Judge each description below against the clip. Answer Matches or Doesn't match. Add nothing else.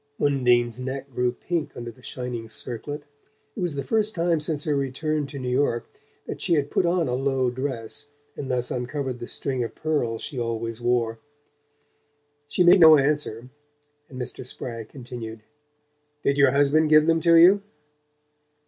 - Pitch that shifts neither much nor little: Matches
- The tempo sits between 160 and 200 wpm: Matches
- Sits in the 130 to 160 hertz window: Matches